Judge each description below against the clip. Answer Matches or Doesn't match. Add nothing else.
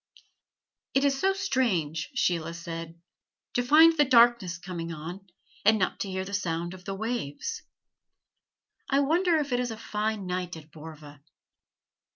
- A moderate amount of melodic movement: Doesn't match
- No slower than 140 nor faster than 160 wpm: Matches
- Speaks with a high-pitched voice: Matches